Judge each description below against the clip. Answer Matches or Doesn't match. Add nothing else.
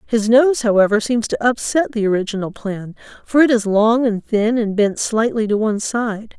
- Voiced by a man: Doesn't match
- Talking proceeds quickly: Doesn't match